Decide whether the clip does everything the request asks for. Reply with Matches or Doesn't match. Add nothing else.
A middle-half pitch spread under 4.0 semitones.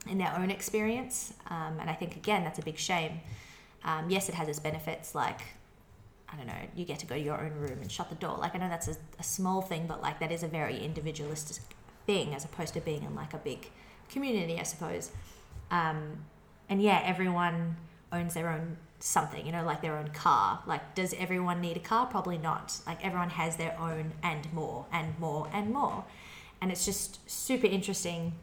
Matches